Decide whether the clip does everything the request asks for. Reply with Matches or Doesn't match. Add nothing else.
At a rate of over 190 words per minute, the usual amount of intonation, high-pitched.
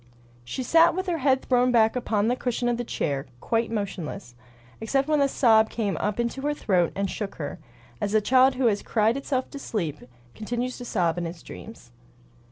Matches